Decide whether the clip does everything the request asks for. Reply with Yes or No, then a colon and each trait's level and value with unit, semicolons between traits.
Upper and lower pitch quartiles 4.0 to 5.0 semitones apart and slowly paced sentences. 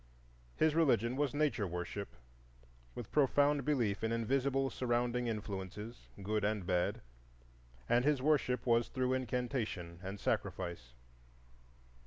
Yes: average, 4.7 semitones; slow, 115 wpm